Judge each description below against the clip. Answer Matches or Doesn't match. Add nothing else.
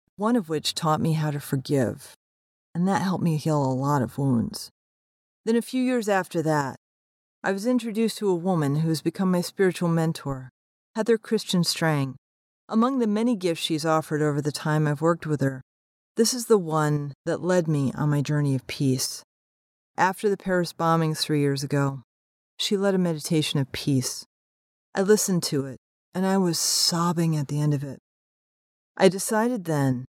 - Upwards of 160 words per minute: Matches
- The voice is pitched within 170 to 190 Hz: Doesn't match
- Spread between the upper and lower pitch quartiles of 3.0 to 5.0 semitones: Doesn't match